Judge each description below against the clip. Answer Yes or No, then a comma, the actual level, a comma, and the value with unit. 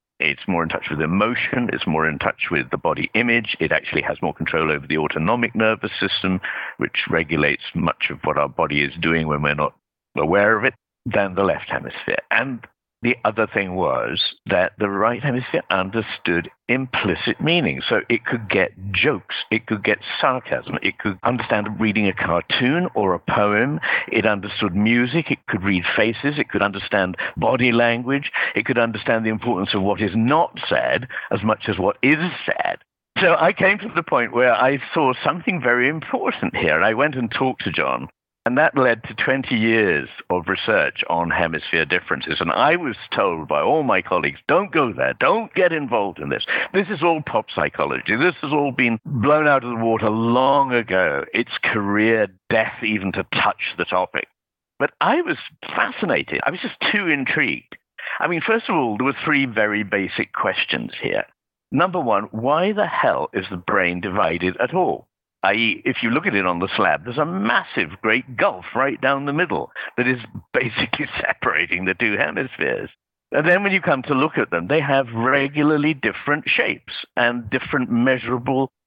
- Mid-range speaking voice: No, low, 115 Hz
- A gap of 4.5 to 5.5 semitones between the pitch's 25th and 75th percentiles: Yes, average, 5.0 semitones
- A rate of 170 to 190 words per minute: Yes, average, 185 wpm